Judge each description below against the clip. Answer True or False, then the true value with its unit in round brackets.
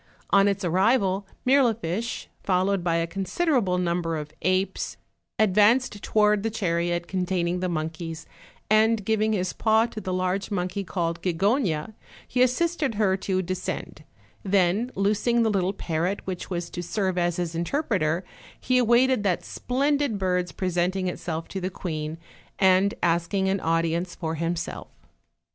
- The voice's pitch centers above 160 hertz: True (185 Hz)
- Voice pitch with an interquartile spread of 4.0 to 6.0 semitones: False (3.6 semitones)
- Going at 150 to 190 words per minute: True (155 wpm)